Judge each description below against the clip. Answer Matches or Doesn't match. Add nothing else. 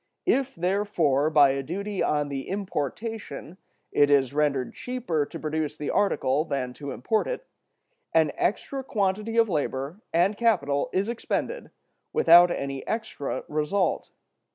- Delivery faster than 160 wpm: Doesn't match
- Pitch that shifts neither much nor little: Doesn't match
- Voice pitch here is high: Doesn't match